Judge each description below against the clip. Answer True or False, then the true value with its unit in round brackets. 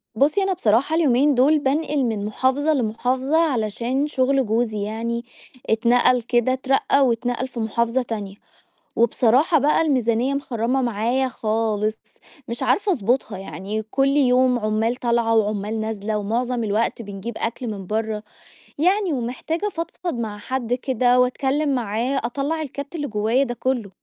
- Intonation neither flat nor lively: True (3.5 semitones)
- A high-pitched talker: True (245 Hz)